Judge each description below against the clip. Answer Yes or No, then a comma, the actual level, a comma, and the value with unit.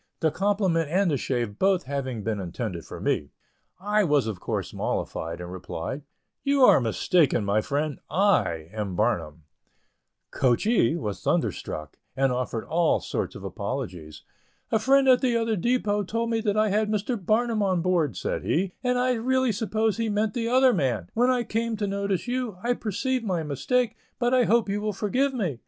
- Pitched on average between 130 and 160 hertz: No, high, 195 Hz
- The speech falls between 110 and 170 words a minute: No, average, 180 wpm